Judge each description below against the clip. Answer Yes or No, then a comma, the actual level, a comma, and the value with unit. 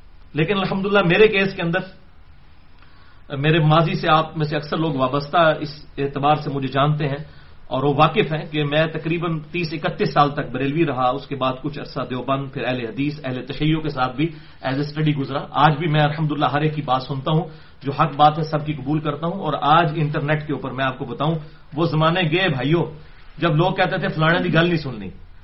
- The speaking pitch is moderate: Yes, medium, 150 Hz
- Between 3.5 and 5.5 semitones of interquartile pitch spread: No, average, 2.8 semitones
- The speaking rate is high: Yes, fast, 220 wpm